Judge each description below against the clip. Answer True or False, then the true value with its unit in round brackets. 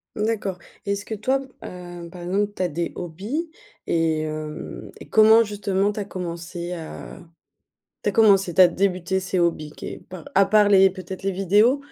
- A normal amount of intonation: True (3.0 semitones)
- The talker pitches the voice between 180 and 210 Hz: True (190 Hz)